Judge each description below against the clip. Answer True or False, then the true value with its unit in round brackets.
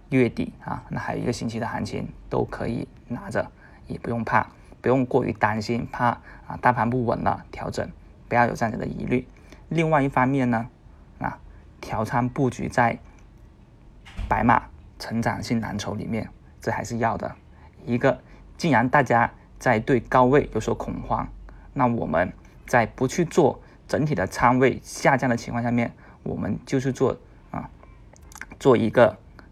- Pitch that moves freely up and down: False (2.7 semitones)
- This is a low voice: True (120 Hz)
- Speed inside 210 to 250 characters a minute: True (230 characters per minute)